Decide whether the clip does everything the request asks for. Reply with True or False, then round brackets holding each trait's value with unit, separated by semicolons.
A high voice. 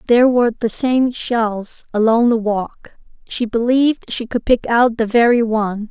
True (230 Hz)